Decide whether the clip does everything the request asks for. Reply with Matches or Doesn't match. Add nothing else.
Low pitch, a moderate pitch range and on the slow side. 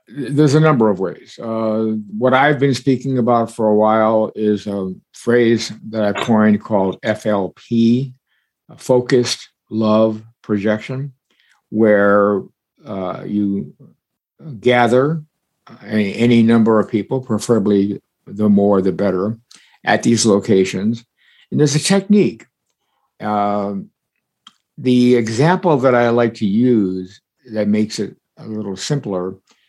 Matches